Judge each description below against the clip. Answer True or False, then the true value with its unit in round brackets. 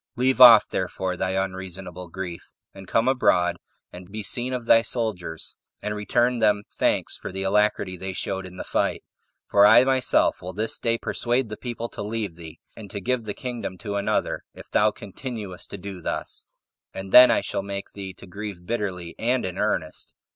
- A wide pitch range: False (3.7 semitones)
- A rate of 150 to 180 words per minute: False (190 wpm)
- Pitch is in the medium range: False (100 Hz)